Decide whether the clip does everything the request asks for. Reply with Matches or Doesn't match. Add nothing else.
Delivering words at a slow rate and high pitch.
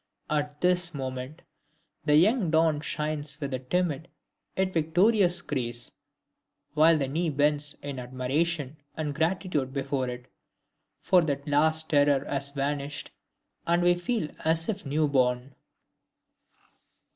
Doesn't match